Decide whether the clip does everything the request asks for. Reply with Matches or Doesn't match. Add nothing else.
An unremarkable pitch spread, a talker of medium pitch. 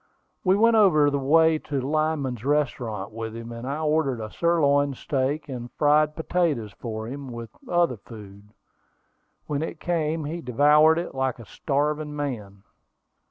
Matches